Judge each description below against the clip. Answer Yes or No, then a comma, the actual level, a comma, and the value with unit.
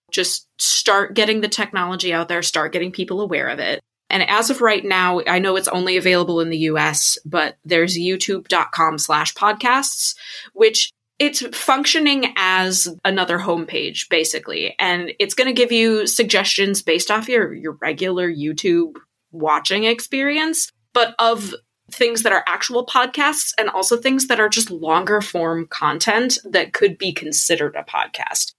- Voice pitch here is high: Yes, high, 195 Hz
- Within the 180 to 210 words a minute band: No, average, 155 wpm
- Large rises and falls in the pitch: Yes, wide, 5.8 semitones